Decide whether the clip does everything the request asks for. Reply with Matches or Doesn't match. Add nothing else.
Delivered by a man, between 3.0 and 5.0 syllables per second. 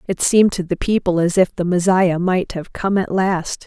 Doesn't match